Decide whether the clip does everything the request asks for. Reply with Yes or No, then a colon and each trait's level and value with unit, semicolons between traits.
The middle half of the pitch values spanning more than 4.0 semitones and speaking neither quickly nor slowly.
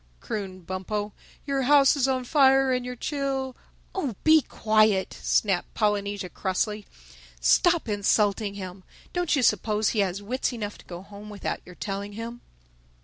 Yes: average, 4.7 semitones; average, 150 wpm